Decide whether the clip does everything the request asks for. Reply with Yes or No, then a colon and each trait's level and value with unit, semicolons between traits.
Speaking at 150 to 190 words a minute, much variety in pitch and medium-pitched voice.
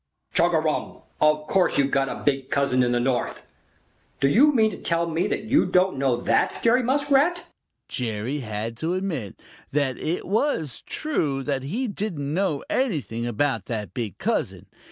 Yes: average, 165 wpm; wide, 7.3 semitones; medium, 150 Hz